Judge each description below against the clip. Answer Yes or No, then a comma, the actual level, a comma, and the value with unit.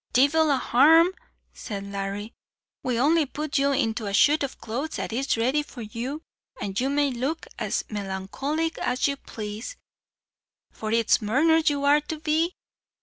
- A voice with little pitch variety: No, average, 5.2 semitones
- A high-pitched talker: Yes, very high, 270 Hz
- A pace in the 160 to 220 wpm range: Yes, average, 165 wpm